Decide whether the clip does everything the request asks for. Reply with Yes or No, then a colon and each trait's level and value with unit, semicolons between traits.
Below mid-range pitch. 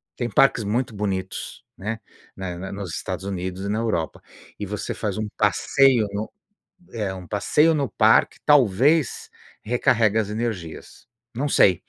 Yes: low, 105 Hz